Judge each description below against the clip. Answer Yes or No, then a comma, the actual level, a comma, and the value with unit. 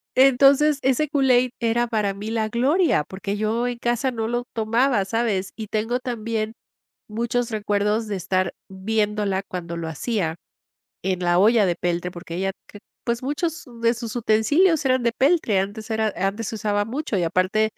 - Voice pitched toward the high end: Yes, high, 220 Hz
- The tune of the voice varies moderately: Yes, average, 3.6 semitones